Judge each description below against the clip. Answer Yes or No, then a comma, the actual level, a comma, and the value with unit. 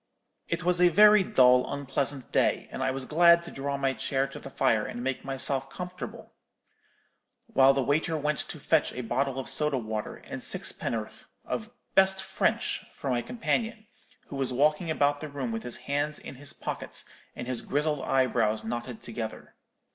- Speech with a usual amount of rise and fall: Yes, average, 3.5 semitones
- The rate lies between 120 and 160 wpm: No, average, 180 wpm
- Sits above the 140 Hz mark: No, low, 135 Hz